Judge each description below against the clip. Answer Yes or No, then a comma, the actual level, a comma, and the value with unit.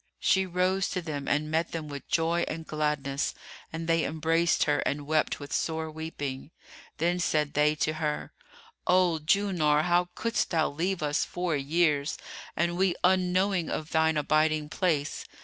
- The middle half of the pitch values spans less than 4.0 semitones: Yes, narrow, 2.6 semitones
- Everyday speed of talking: Yes, average, 160 wpm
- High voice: No, medium, 160 Hz